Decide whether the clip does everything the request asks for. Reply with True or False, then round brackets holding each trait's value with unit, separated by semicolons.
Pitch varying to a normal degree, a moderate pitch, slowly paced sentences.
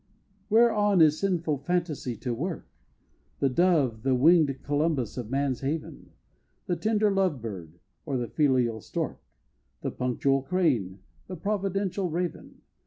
False (6.1 semitones; 150 Hz; 130 wpm)